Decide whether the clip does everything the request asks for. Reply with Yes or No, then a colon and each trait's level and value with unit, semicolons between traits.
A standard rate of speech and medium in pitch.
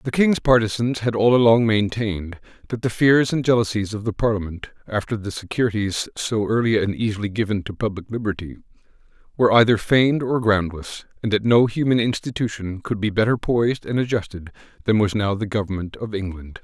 No: average, 175 wpm; low, 110 Hz